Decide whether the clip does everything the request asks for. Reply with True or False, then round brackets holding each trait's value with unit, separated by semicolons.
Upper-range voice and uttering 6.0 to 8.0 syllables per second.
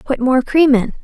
False (265 Hz; 4.8 syllables/s)